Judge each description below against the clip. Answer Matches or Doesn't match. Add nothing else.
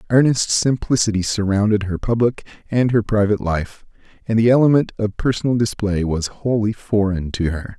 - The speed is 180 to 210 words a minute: Doesn't match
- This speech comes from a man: Matches